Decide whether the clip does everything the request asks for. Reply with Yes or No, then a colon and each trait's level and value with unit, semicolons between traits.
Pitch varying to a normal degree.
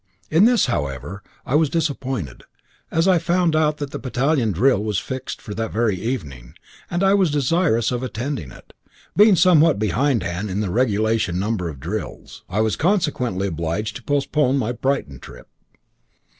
No: wide, 7.1 semitones